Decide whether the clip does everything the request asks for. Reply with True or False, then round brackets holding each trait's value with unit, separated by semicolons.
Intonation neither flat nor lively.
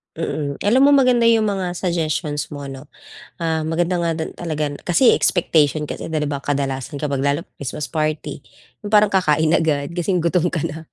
True (3.6 semitones)